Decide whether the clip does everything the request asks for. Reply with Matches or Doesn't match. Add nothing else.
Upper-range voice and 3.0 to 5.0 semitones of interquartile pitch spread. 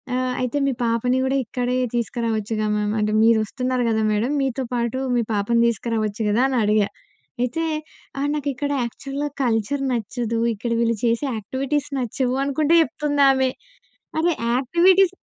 Matches